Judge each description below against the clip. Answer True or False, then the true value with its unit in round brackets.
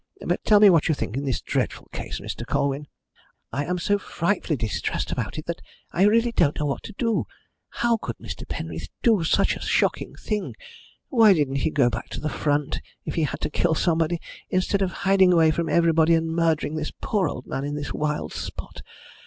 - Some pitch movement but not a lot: True (4.7 semitones)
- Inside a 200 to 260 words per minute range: True (205 wpm)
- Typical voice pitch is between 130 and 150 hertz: False (165 Hz)